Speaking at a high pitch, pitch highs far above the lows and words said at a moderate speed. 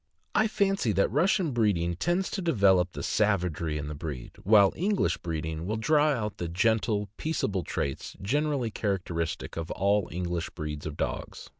No: low, 100 Hz; wide, 8.4 semitones; average, 170 wpm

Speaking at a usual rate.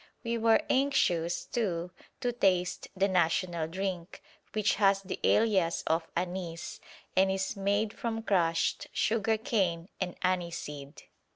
No: slow, 125 wpm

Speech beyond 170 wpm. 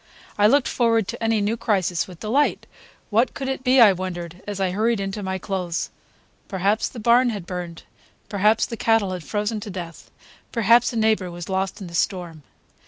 Yes: average, 190 wpm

